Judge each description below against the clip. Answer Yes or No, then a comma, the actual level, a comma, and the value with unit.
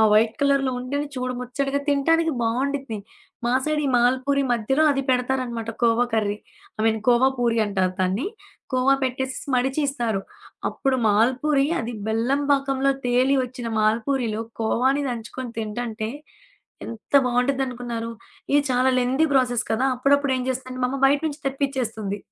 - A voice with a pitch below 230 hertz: No, very high, 255 Hz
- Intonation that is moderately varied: Yes, average, 3.0 semitones